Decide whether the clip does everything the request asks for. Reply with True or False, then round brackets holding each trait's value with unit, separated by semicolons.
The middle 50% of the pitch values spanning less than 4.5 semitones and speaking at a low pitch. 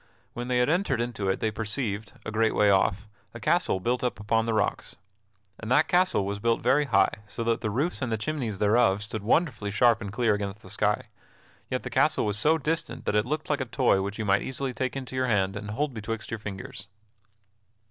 True (3.8 semitones; 115 Hz)